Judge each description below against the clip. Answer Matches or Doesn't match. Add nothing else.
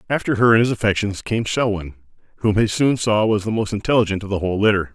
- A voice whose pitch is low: Matches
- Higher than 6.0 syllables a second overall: Matches